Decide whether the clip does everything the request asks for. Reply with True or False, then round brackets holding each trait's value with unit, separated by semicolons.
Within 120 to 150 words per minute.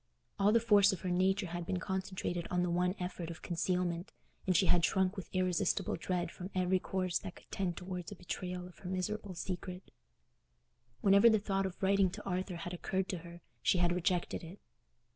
False (200 wpm)